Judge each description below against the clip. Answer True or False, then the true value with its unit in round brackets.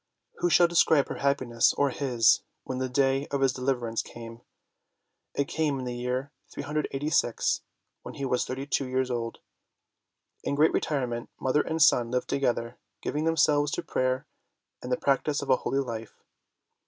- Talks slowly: False (165 wpm)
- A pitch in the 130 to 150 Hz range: True (135 Hz)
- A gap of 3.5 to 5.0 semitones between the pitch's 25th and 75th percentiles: False (2.4 semitones)